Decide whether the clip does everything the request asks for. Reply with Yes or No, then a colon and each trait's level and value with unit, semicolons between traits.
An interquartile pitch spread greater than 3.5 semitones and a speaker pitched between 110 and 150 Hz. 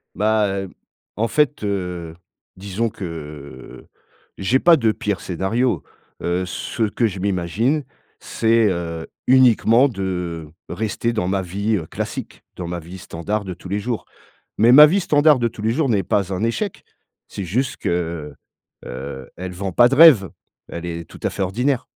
No: average, 4.8 semitones; low, 100 Hz